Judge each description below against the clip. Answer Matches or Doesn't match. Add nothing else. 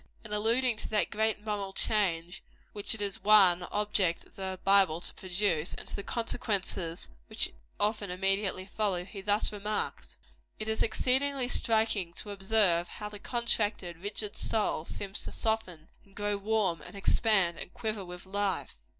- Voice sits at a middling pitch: Doesn't match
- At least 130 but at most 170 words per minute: Matches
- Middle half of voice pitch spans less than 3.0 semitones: Matches